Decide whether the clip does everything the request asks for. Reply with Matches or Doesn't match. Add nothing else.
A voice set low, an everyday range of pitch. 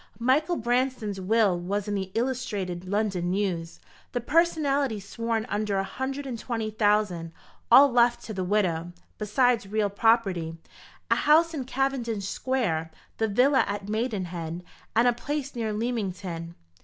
Doesn't match